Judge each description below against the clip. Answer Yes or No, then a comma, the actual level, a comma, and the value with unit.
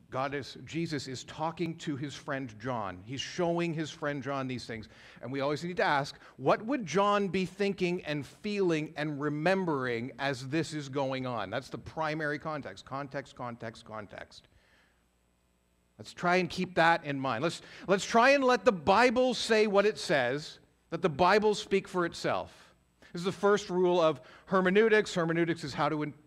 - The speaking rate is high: No, average, 180 wpm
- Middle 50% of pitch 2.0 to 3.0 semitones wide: No, average, 5.3 semitones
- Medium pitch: Yes, medium, 155 Hz